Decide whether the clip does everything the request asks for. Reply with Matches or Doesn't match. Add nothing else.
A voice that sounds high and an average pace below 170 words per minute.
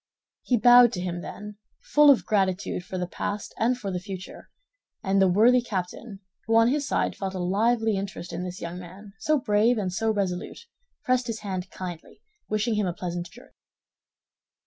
Doesn't match